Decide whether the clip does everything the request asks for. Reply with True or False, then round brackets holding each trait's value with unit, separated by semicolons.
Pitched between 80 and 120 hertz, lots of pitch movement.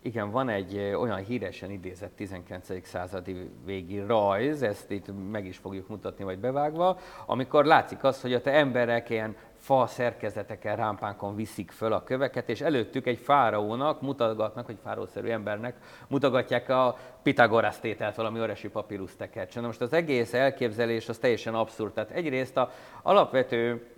False (115 Hz; 3.8 semitones)